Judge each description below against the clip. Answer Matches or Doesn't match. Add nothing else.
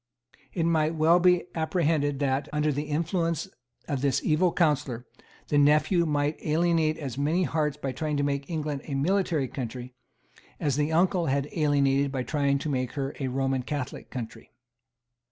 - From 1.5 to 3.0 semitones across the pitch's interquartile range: Matches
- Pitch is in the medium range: Matches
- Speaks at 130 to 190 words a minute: Matches